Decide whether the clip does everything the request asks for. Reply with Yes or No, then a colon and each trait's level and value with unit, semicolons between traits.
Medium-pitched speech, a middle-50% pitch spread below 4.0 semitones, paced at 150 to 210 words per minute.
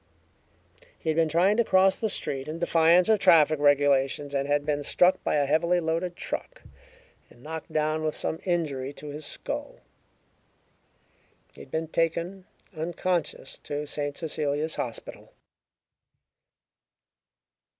No: medium, 155 Hz; average, 2.9 semitones; slow, 135 wpm